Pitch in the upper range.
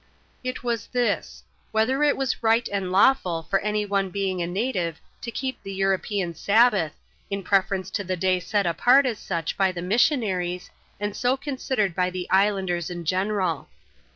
Yes: high, 195 Hz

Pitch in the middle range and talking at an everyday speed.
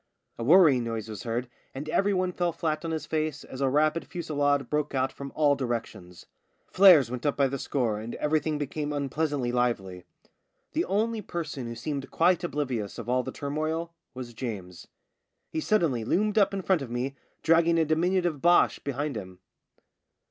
Yes: medium, 145 Hz; average, 175 wpm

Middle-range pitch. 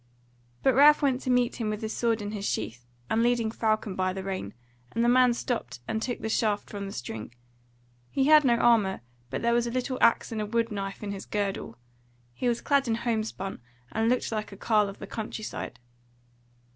No: high, 220 Hz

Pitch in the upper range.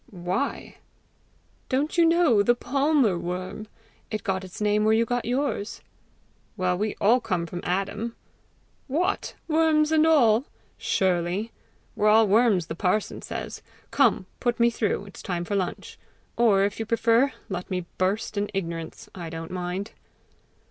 Yes: high, 210 Hz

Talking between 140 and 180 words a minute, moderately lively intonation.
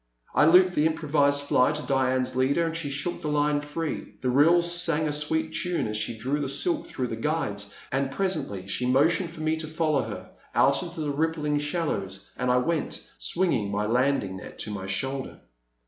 No: average, 195 wpm; average, 4.2 semitones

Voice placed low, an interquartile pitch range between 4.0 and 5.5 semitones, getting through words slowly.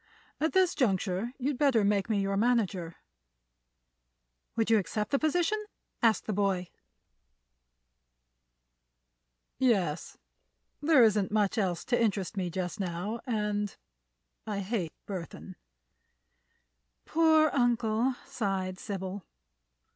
No: high, 210 Hz; average, 4.3 semitones; slow, 100 wpm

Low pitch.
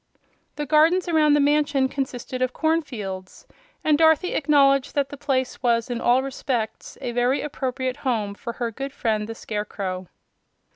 No: very high, 260 Hz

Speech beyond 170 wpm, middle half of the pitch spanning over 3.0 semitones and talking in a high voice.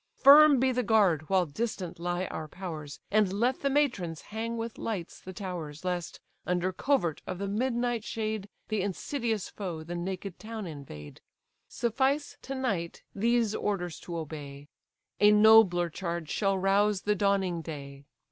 No: average, 155 wpm; average, 4.6 semitones; high, 195 Hz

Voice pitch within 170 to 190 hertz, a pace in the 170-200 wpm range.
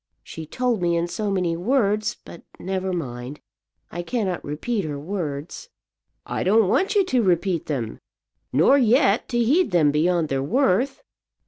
No: medium, 185 Hz; average, 155 wpm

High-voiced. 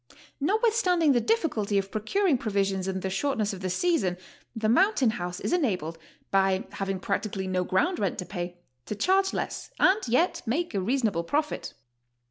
Yes: high, 215 Hz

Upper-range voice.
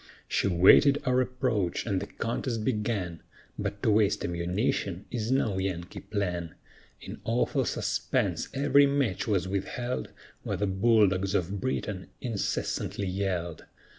No: low, 100 Hz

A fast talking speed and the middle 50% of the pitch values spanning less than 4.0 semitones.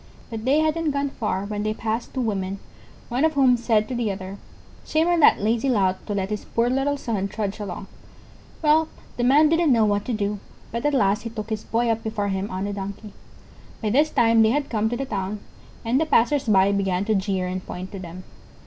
No: fast, 230 wpm; average, 4.5 semitones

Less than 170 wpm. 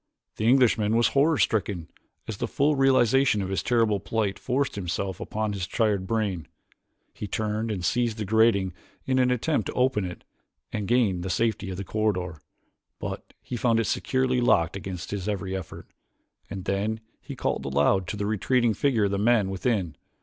No: average, 180 wpm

